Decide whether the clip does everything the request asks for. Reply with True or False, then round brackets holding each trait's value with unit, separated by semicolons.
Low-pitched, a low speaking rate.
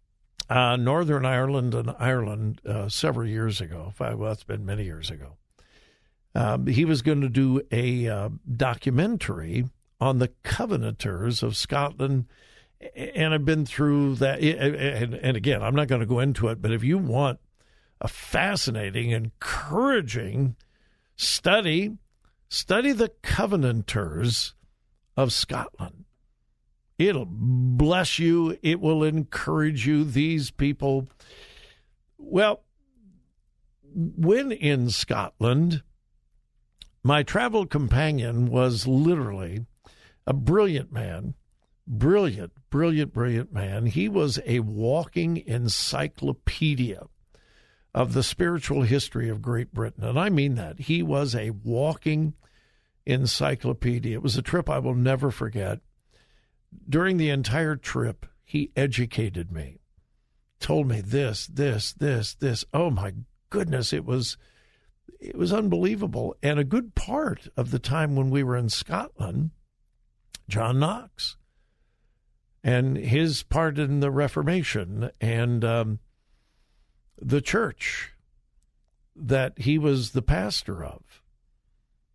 True (130 Hz; 120 wpm)